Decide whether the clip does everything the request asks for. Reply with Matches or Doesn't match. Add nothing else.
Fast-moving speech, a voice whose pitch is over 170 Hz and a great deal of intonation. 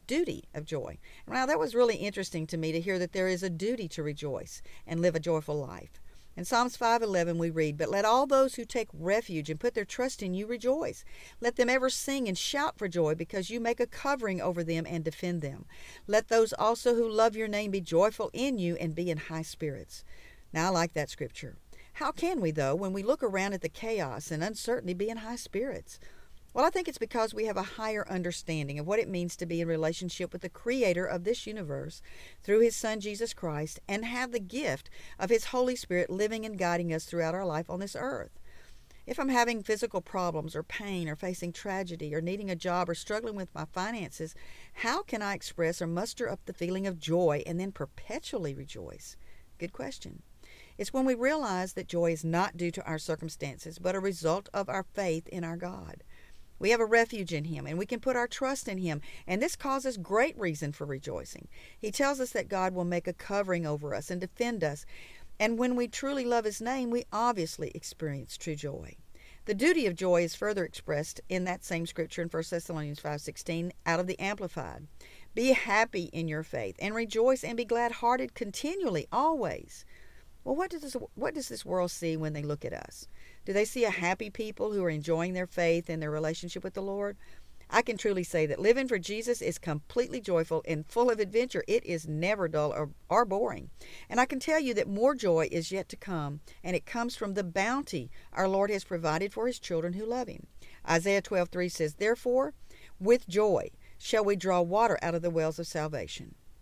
Matches